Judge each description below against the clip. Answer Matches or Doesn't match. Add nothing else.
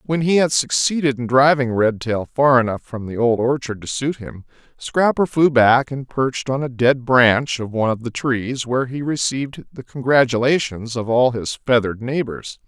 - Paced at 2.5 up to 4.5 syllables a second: Doesn't match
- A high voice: Doesn't match